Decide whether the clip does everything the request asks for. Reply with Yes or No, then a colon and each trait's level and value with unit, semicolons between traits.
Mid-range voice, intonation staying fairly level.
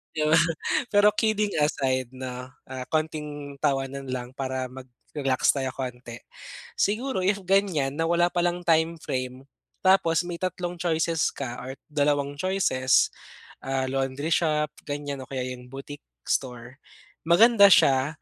No: medium, 145 Hz; average, 4.7 semitones